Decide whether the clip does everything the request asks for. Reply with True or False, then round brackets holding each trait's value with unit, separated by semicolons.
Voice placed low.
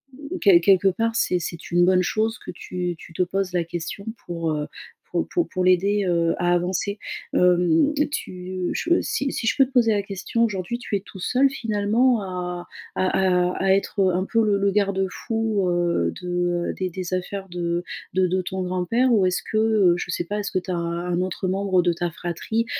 False (185 Hz)